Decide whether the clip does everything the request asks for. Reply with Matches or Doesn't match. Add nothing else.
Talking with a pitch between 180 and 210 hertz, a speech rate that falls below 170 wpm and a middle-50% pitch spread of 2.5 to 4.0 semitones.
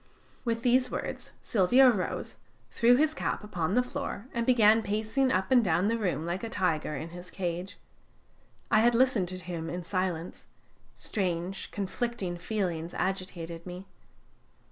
Doesn't match